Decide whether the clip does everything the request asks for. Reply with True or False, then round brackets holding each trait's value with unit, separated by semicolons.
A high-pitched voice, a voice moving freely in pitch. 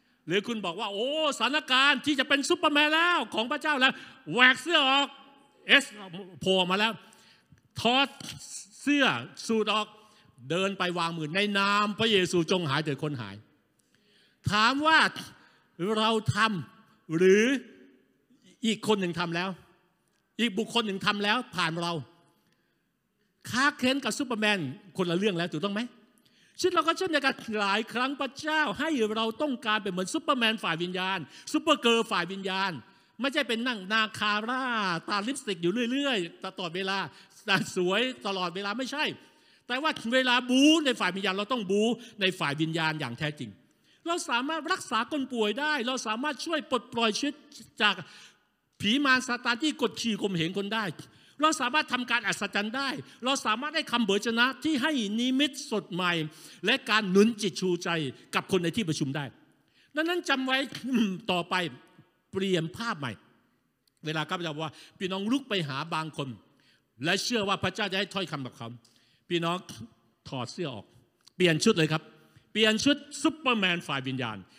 True (210 Hz; 6.3 semitones)